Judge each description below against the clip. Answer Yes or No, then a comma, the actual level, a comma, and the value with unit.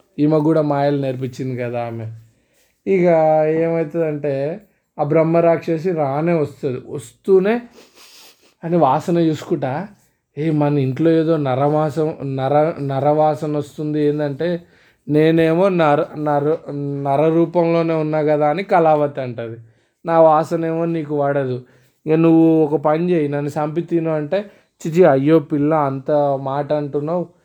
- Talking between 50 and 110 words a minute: No, average, 120 wpm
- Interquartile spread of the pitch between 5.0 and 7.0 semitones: No, narrow, 2.4 semitones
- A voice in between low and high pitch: Yes, medium, 155 Hz